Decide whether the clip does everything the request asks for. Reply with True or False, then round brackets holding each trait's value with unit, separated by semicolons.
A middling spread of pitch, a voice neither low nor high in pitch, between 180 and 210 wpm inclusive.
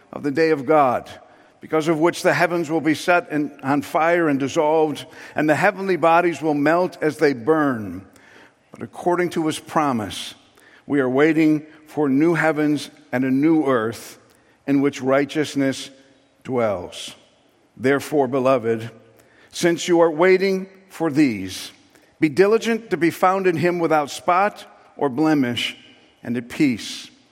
False (3.8 semitones; 155 Hz; 150 wpm)